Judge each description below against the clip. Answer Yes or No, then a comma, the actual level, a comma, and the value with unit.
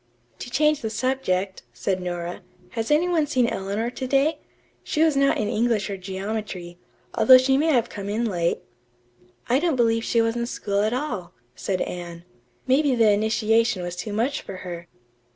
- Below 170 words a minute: No, average, 180 wpm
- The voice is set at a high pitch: Yes, high, 225 Hz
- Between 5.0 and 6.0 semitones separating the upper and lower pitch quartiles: Yes, average, 5.3 semitones